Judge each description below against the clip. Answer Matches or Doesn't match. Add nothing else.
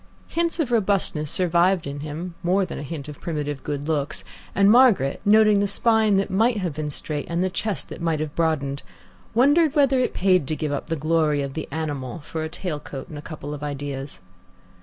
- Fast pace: Matches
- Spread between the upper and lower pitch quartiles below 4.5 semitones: Doesn't match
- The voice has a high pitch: Doesn't match